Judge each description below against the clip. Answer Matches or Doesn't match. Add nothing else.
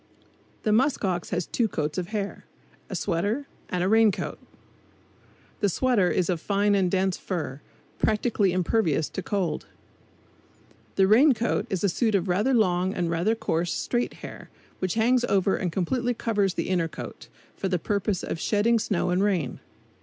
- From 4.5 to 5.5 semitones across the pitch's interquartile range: Doesn't match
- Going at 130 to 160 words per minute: Doesn't match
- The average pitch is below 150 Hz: Doesn't match